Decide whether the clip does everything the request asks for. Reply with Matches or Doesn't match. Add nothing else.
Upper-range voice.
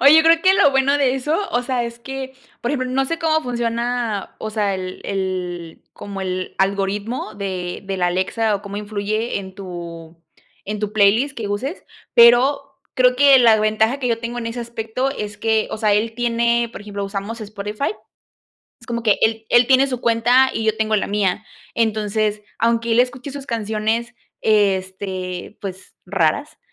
Matches